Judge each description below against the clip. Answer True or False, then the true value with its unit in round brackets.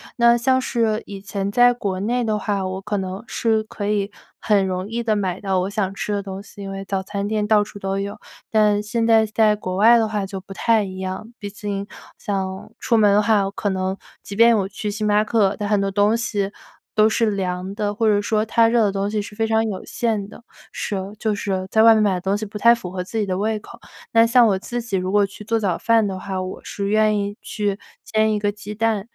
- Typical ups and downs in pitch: False (2.0 semitones)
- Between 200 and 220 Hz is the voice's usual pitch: True (205 Hz)